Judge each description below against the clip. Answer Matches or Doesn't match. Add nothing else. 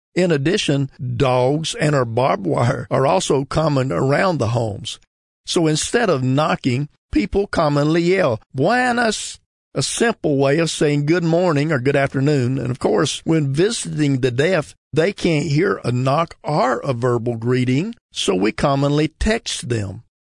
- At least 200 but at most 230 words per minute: Doesn't match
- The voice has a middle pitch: Matches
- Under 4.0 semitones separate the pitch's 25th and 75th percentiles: Doesn't match